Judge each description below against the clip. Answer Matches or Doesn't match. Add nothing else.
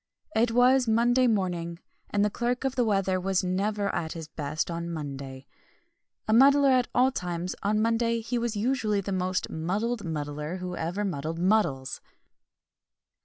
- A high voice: Matches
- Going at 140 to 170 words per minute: Matches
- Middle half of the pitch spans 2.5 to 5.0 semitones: Doesn't match